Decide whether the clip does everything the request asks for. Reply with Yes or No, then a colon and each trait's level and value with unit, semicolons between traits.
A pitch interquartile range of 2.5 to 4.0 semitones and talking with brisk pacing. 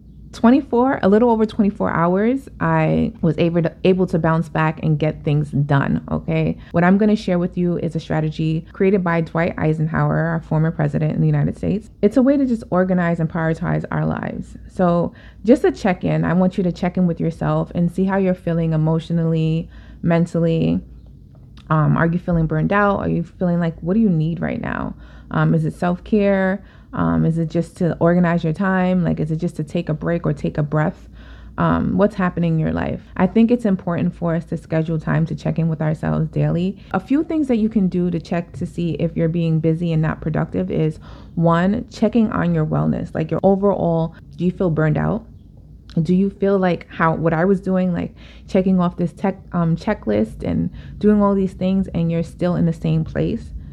Yes: average, 3.1 semitones; fast, 215 wpm